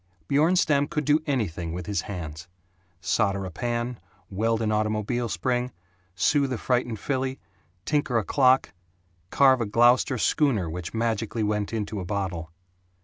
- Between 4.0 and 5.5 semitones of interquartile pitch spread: Yes, average, 4.7 semitones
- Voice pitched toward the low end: Yes, low, 115 Hz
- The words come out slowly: No, average, 145 wpm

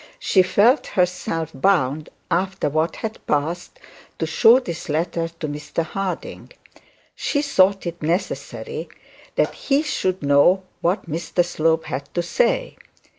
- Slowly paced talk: Yes, slow, 130 wpm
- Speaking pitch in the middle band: Yes, medium, 175 Hz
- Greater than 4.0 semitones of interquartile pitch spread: No, average, 3.4 semitones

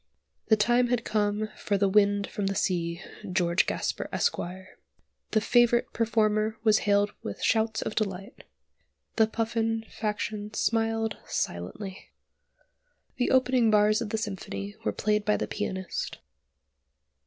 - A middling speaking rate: No, slow, 130 wpm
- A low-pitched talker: No, high, 215 Hz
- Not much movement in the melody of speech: Yes, narrow, 1.9 semitones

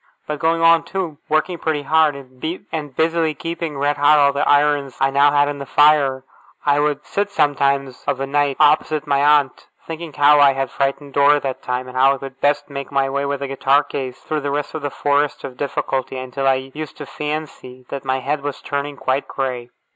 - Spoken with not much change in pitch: Yes, narrow, 1.6 semitones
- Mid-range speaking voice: Yes, medium, 145 Hz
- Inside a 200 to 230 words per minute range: Yes, fast, 205 wpm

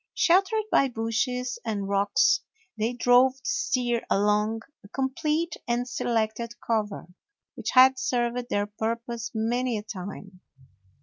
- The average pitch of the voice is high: Yes, high, 235 Hz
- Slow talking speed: Yes, slow, 125 wpm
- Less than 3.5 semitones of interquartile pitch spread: Yes, average, 2.8 semitones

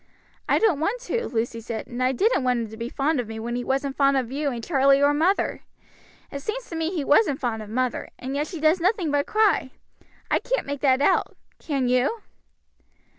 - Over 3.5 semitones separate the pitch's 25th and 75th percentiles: Yes, average, 4.7 semitones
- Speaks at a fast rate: Yes, fast, 225 wpm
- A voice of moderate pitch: No, very high, 275 Hz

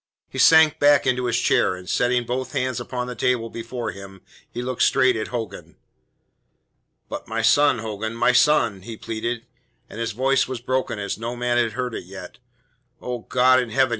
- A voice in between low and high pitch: No, low, 120 Hz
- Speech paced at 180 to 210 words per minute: Yes, average, 190 wpm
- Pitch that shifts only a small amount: Yes, narrow, 2.2 semitones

